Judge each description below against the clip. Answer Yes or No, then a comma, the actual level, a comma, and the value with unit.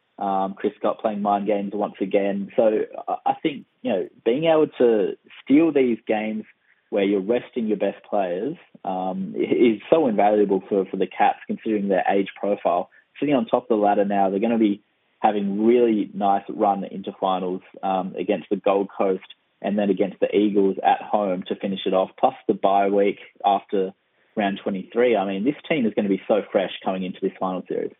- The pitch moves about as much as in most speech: No, narrow, 2.1 semitones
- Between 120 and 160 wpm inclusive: No, average, 195 wpm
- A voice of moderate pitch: No, low, 100 Hz